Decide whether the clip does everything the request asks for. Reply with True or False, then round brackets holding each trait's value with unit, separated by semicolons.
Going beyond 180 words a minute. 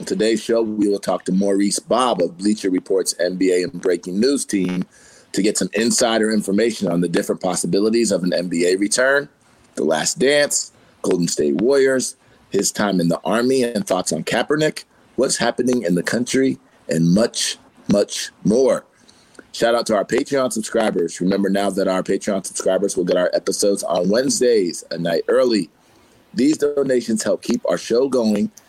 False (170 wpm)